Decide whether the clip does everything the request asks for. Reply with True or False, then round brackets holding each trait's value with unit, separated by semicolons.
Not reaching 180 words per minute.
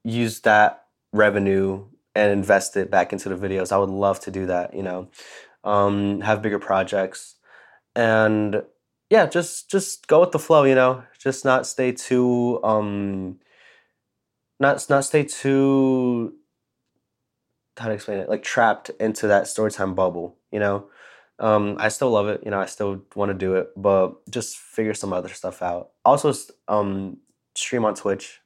True (165 wpm)